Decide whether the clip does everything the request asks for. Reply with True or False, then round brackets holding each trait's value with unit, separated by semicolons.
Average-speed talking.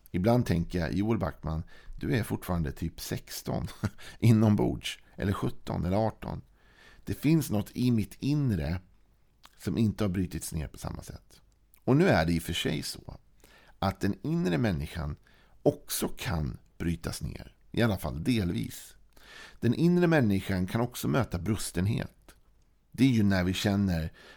True (160 wpm)